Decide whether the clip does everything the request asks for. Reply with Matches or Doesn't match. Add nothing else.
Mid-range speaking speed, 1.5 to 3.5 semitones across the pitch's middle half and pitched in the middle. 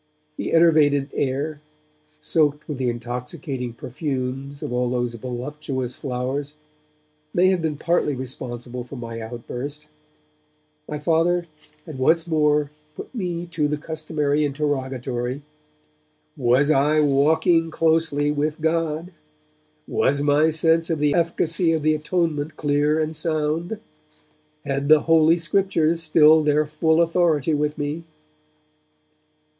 Doesn't match